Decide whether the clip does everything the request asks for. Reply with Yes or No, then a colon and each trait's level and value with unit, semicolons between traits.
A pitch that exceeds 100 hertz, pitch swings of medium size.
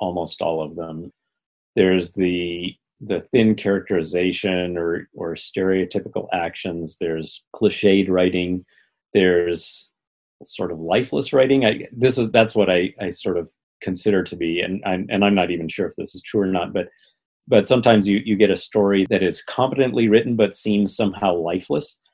No: very low, 95 Hz; average, 3.2 semitones